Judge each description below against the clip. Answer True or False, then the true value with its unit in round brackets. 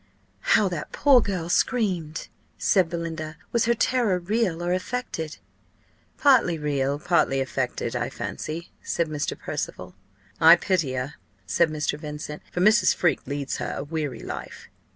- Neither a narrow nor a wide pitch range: True (4.4 semitones)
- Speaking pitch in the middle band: True (170 Hz)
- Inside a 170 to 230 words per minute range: False (145 wpm)